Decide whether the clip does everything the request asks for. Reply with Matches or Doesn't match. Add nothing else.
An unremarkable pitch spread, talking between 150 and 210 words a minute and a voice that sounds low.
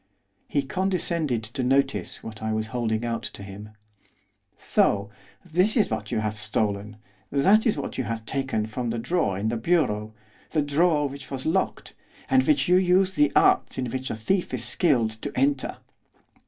Doesn't match